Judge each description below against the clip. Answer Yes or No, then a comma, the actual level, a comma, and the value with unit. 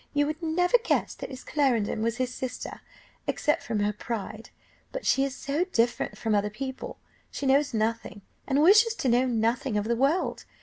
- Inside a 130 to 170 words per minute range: No, average, 185 wpm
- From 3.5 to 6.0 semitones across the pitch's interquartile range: Yes, average, 4.6 semitones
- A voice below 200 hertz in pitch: No, very high, 260 Hz